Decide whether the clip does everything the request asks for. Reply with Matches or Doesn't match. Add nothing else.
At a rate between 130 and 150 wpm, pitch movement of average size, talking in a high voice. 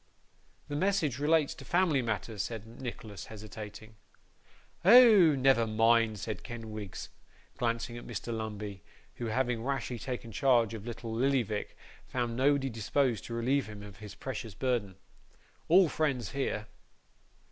Doesn't match